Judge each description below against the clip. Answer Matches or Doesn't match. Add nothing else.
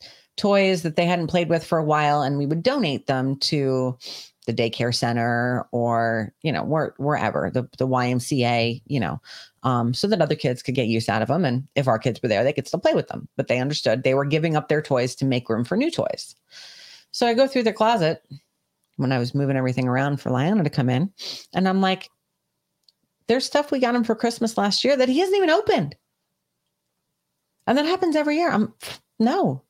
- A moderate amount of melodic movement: Doesn't match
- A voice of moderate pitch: Matches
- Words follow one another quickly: Matches